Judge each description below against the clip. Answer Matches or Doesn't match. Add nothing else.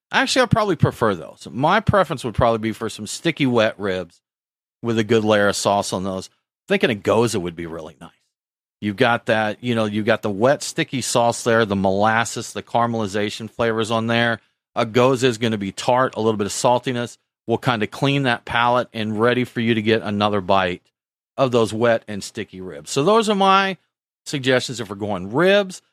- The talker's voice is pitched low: Matches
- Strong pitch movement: Doesn't match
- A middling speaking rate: Doesn't match